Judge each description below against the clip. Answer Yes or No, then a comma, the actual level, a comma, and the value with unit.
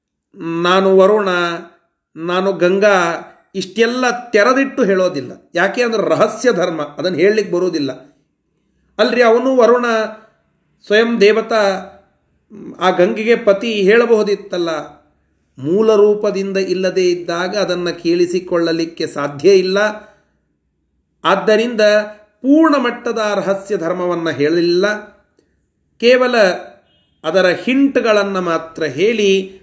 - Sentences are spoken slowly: No, average, 85 wpm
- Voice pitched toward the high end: Yes, high, 195 Hz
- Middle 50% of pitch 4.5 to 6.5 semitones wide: No, average, 3.6 semitones